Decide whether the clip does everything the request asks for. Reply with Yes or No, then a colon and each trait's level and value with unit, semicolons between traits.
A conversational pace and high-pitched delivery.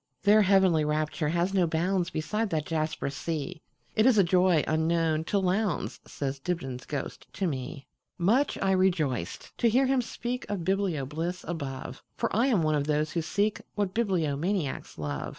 No: average, 145 wpm; medium, 170 Hz